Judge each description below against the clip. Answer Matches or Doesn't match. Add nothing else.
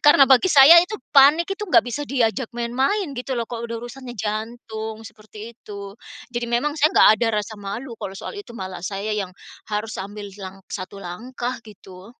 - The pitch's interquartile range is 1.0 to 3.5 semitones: Doesn't match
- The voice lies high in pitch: Matches